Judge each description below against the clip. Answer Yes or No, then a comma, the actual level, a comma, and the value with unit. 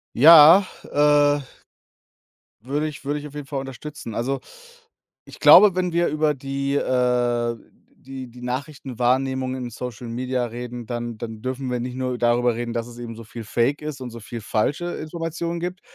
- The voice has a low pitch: Yes, low, 130 Hz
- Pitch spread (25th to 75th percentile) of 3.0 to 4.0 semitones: Yes, average, 3.4 semitones